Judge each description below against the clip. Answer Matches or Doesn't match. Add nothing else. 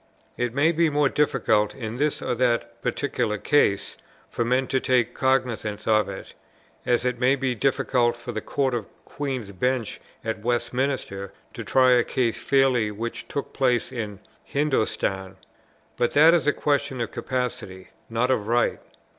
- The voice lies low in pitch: Matches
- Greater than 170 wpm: Doesn't match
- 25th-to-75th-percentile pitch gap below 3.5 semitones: Matches